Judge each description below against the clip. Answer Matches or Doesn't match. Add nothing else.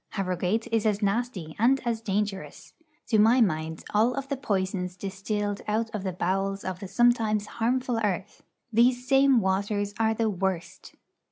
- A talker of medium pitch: Doesn't match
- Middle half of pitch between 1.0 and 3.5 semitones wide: Matches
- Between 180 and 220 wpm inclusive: Doesn't match